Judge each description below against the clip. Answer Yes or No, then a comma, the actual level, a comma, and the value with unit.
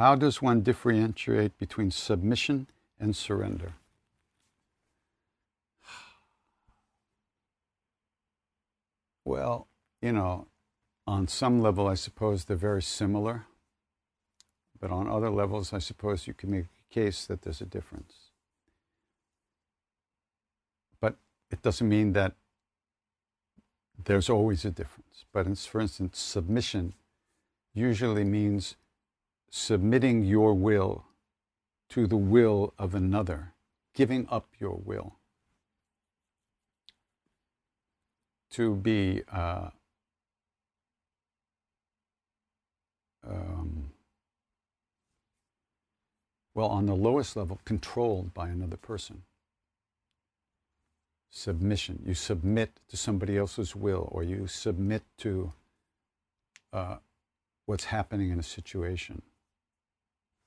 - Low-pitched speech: Yes, low, 100 Hz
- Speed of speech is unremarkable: No, slow, 90 wpm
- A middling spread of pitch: Yes, average, 3.1 semitones